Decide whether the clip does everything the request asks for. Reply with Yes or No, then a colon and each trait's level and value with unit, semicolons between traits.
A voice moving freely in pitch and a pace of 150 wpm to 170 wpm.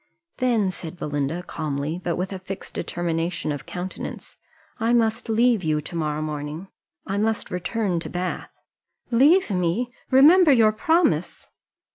No: wide, 5.7 semitones; average, 140 wpm